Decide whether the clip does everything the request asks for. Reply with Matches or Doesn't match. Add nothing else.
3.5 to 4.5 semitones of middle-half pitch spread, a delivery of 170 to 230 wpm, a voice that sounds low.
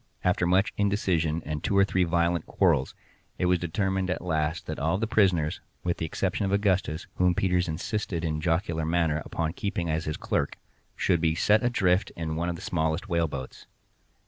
Doesn't match